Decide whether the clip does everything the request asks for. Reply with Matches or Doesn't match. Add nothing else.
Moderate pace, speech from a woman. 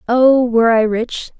Matches